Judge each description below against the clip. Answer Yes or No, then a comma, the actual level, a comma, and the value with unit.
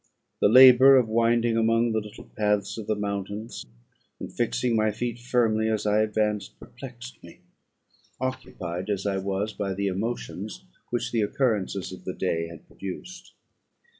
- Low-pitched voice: Yes, low, 110 Hz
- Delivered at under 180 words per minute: Yes, average, 155 wpm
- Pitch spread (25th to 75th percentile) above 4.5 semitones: No, average, 3.1 semitones